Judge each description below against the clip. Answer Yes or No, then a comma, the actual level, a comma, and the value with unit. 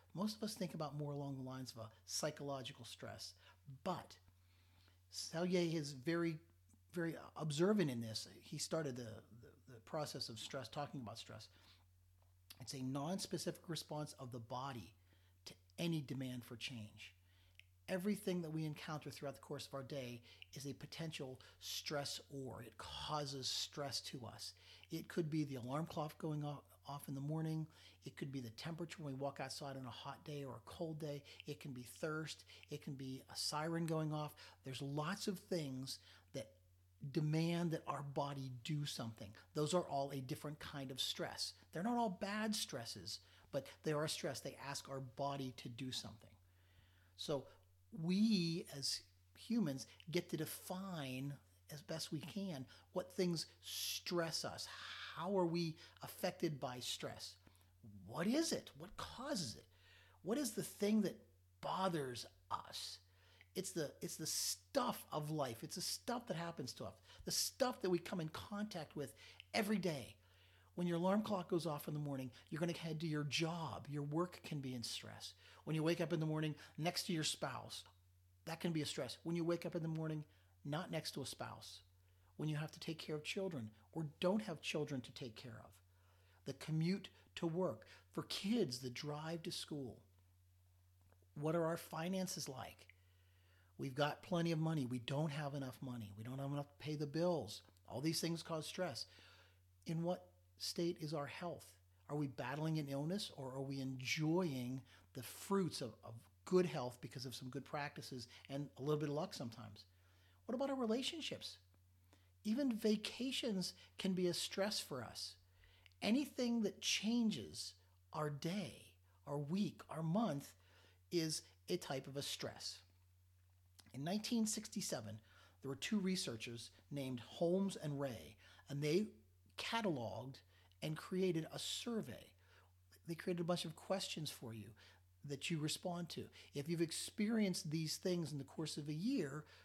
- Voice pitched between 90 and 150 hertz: Yes, medium, 140 Hz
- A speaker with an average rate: Yes, average, 170 wpm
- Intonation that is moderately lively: No, wide, 9.0 semitones